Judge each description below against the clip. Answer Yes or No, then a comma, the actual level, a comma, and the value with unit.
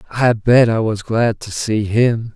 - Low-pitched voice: Yes, low, 115 Hz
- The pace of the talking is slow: No, fast, 205 wpm